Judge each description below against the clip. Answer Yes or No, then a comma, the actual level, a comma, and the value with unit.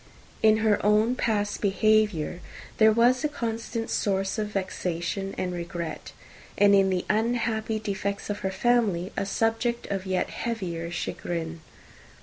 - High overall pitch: Yes, high, 205 Hz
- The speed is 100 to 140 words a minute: Yes, slow, 135 wpm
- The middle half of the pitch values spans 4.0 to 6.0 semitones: No, average, 3.1 semitones